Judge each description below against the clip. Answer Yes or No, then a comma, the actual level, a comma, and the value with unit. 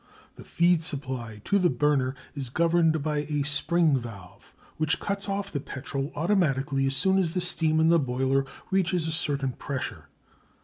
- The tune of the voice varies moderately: Yes, average, 4.0 semitones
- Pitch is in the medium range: Yes, medium, 150 Hz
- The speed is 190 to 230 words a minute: No, average, 170 wpm